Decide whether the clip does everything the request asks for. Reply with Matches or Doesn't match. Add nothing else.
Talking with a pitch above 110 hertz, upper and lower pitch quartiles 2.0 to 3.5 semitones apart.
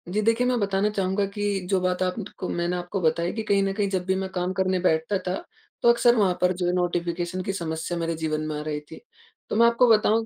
Matches